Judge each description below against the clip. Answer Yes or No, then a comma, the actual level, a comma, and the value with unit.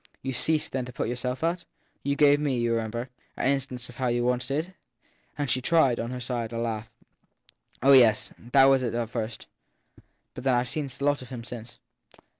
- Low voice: Yes, low, 125 Hz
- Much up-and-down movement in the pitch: No, narrow, 2.6 semitones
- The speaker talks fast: Yes, fast, 215 wpm